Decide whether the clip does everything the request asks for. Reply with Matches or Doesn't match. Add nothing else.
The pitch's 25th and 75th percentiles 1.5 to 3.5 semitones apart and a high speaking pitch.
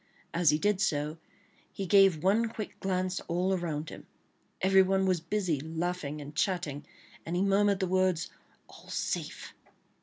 Doesn't match